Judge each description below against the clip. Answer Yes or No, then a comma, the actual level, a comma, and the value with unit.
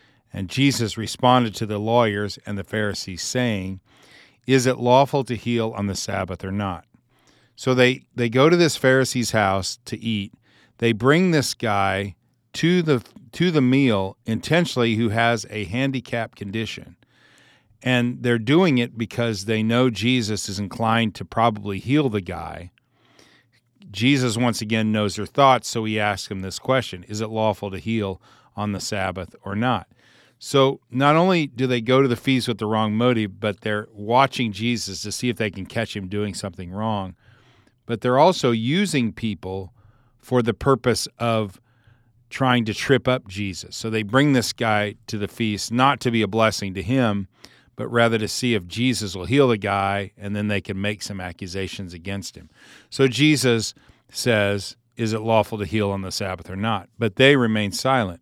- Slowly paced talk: No, average, 180 wpm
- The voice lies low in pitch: Yes, low, 115 Hz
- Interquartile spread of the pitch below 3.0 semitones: No, average, 3.6 semitones